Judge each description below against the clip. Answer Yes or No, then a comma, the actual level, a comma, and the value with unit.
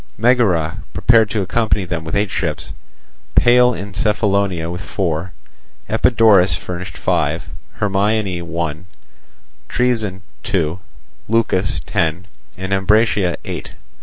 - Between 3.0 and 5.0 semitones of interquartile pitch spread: Yes, average, 3.8 semitones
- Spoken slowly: Yes, slow, 105 wpm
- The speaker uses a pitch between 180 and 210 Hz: No, very low, 95 Hz